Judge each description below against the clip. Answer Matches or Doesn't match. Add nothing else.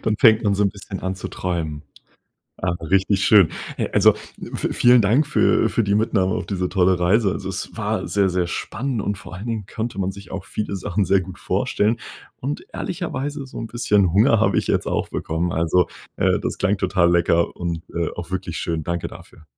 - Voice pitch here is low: Matches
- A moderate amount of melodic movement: Matches